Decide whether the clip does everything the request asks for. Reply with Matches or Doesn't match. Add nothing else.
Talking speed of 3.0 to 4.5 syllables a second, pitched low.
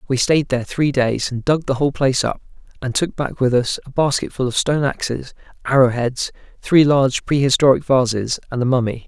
Doesn't match